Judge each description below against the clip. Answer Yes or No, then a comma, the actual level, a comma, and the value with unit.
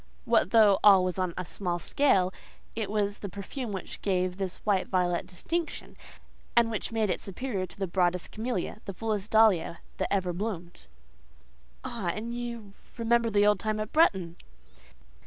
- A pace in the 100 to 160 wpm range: Yes, average, 155 wpm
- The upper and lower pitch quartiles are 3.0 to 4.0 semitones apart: Yes, average, 3.4 semitones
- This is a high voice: Yes, high, 200 Hz